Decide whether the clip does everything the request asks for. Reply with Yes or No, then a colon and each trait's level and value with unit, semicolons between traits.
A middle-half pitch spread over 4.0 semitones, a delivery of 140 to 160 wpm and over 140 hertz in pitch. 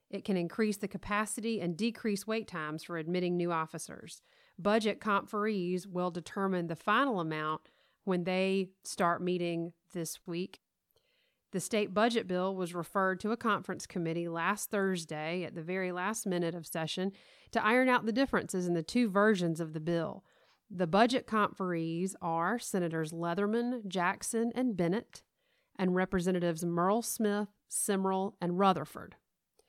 No: average, 3.6 semitones; average, 150 wpm; high, 190 Hz